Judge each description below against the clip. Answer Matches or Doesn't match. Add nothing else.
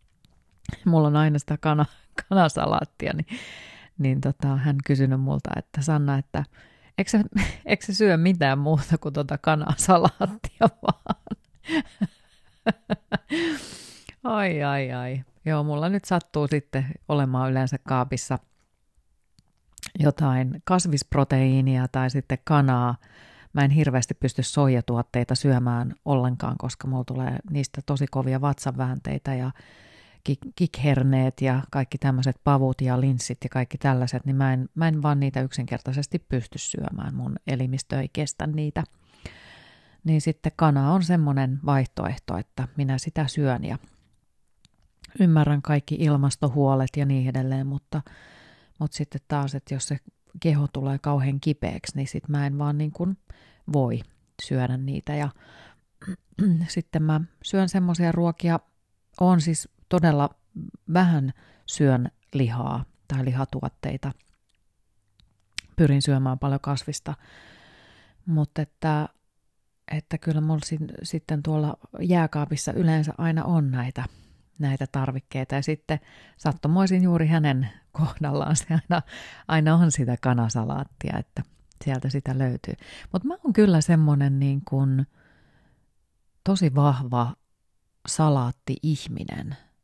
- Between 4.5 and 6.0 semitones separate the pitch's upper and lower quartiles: Doesn't match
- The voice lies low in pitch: Doesn't match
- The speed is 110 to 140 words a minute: Matches